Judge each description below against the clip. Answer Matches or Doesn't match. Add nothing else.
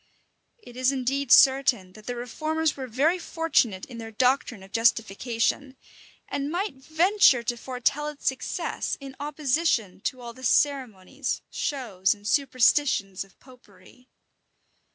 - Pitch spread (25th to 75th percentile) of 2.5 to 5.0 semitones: Matches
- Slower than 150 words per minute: Matches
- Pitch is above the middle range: Matches